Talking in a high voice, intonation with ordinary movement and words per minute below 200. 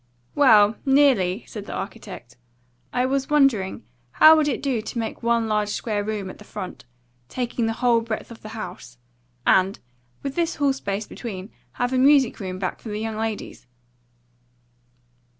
Yes: high, 225 Hz; average, 4.0 semitones; average, 170 wpm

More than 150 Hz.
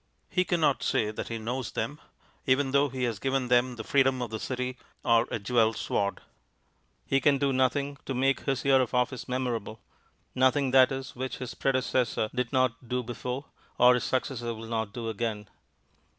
No: low, 125 Hz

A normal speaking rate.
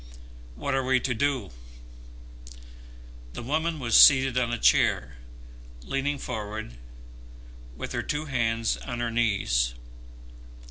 No: slow, 120 wpm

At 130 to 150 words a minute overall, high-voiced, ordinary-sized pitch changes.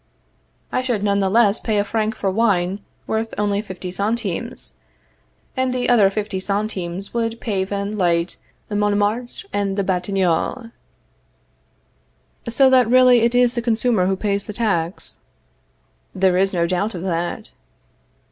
Yes: average, 145 wpm; high, 205 Hz; average, 3.3 semitones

